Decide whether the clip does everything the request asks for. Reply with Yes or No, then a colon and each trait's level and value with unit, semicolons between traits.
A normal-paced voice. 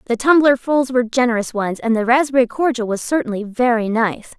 Yes: average, 180 wpm